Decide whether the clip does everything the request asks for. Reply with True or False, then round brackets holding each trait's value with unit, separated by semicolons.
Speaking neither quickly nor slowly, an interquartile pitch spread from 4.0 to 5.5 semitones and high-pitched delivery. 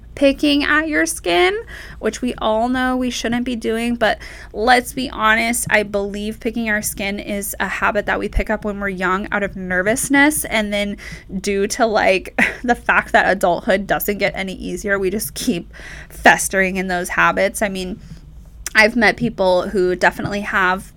False (175 wpm; 3.3 semitones; 210 Hz)